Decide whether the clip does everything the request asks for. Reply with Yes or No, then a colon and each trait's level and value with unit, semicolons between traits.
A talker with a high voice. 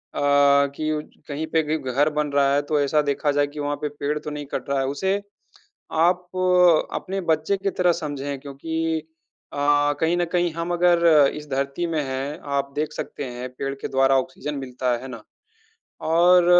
No: medium, 150 Hz